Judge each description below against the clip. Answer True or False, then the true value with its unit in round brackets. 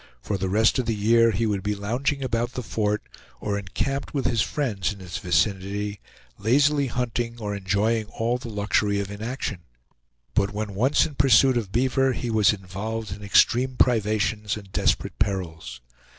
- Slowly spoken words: False (170 wpm)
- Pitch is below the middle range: True (110 Hz)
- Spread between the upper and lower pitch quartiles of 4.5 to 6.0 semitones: False (3.2 semitones)